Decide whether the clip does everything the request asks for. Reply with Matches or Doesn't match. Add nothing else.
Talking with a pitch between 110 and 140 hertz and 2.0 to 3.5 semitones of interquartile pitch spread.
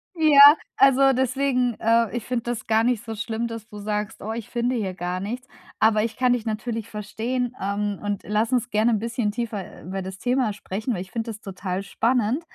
Doesn't match